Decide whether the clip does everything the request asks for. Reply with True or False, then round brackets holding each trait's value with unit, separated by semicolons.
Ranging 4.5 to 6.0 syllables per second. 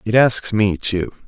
False (3.9 syllables/s)